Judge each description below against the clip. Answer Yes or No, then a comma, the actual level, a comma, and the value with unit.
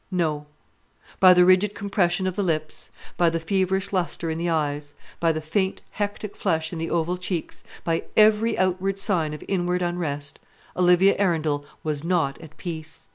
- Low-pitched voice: No, medium, 175 Hz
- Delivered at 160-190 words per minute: Yes, average, 170 wpm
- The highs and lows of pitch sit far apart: No, average, 2.9 semitones